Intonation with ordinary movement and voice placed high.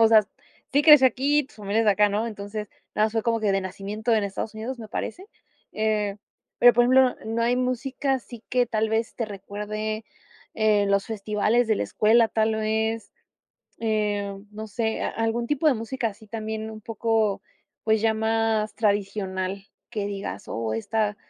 No: narrow, 1.8 semitones; high, 220 Hz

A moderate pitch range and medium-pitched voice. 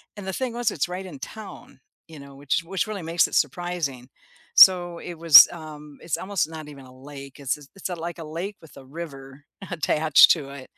Yes: average, 4.0 semitones; medium, 160 Hz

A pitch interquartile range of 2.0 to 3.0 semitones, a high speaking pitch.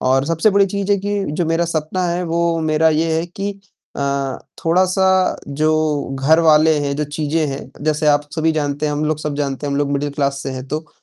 No: narrow, 2.5 semitones; medium, 155 Hz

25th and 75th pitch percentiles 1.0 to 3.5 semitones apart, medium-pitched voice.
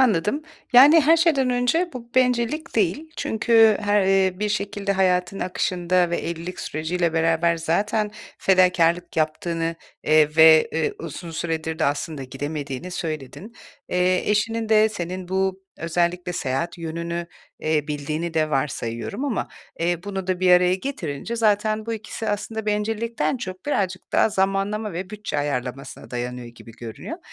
No: average, 4.8 semitones; medium, 180 Hz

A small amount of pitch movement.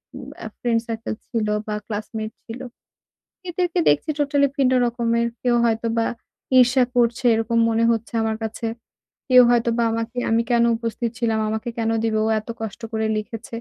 Yes: narrow, 1.3 semitones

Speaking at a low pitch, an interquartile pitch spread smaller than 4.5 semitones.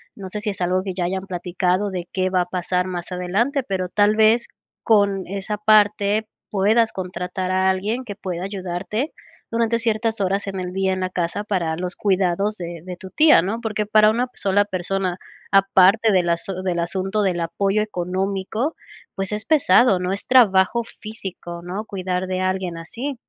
No: high, 195 Hz; average, 2.7 semitones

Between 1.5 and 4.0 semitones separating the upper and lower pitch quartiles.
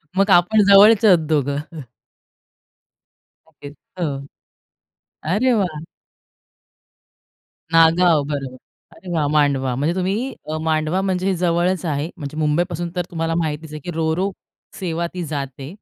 Yes: average, 3.4 semitones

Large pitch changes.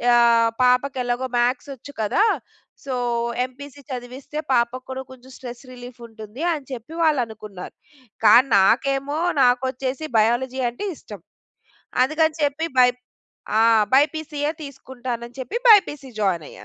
No: average, 2.9 semitones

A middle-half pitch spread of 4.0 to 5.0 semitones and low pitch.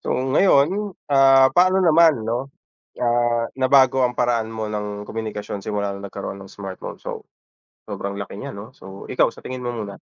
Yes: average, 4.4 semitones; low, 120 Hz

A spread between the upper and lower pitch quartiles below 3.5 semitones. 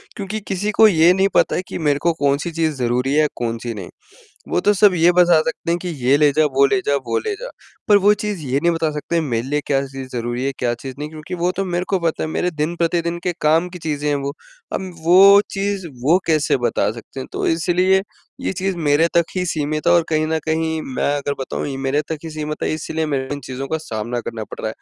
No: average, 4.2 semitones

